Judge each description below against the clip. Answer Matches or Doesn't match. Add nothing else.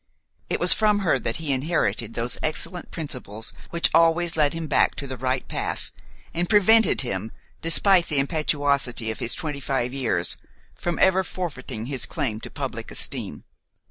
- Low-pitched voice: Doesn't match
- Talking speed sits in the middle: Matches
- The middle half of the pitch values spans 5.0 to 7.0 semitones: Matches